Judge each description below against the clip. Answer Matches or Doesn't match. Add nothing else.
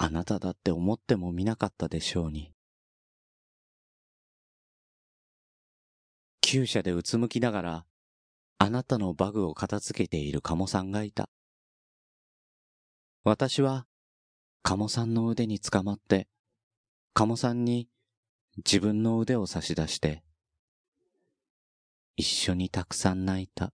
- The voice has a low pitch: Matches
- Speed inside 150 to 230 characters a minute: Matches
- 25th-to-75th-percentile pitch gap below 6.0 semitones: Matches